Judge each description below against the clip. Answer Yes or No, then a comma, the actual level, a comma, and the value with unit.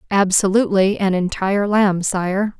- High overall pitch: Yes, high, 195 Hz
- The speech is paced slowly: Yes, slow, 115 wpm